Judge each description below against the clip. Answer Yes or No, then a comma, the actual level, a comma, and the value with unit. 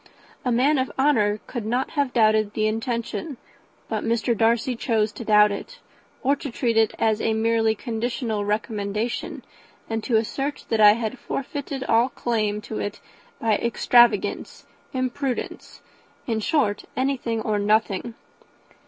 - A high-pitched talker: Yes, high, 230 Hz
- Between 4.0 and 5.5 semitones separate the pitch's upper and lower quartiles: No, average, 2.8 semitones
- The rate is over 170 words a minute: No, average, 145 wpm